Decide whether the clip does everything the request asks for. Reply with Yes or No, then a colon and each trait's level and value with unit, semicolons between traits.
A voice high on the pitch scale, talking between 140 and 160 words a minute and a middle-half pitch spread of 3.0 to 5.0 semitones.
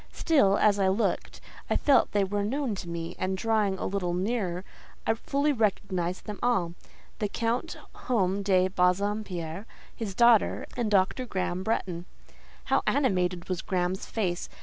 Yes: high, 195 Hz; average, 150 wpm; average, 3.5 semitones